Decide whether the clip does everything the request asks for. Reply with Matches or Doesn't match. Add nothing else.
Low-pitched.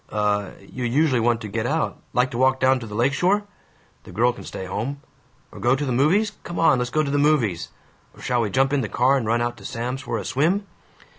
Matches